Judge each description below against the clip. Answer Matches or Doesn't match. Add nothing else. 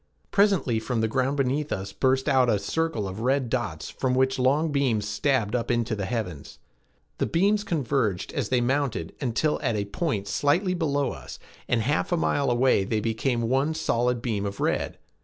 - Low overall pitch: Matches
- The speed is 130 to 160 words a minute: Doesn't match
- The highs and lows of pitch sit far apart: Doesn't match